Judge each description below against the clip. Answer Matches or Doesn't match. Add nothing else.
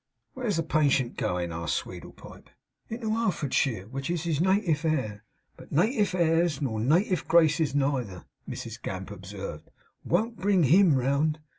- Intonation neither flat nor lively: Doesn't match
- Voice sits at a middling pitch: Matches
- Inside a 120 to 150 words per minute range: Matches